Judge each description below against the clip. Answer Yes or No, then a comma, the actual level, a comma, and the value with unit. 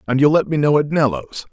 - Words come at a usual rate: No, fast, 275 wpm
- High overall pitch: No, medium, 140 Hz